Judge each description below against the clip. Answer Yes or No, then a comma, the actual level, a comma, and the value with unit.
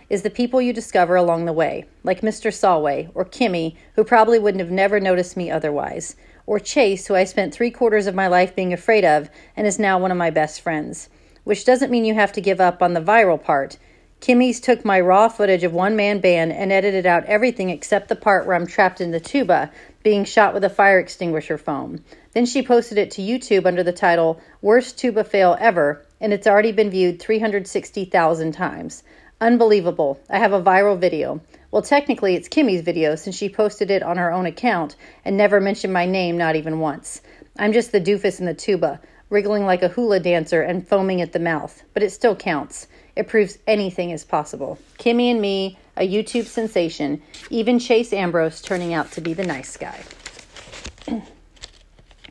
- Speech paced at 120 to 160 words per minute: No, average, 195 wpm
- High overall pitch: Yes, high, 195 Hz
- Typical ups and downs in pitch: Yes, average, 3.6 semitones